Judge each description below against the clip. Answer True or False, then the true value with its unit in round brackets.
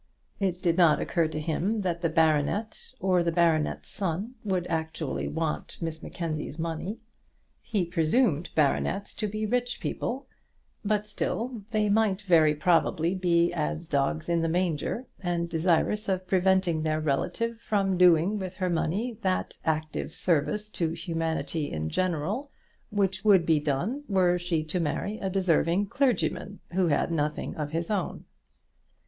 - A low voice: False (175 Hz)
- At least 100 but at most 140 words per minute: False (150 wpm)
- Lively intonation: False (3.9 semitones)